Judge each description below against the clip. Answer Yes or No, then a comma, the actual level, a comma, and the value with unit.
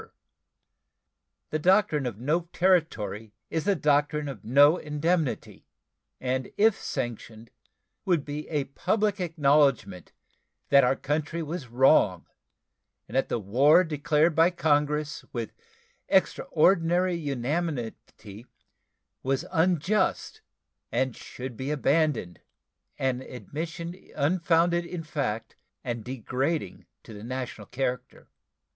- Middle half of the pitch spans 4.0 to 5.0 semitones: Yes, average, 4.7 semitones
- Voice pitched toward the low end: No, medium, 145 Hz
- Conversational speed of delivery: No, slow, 105 wpm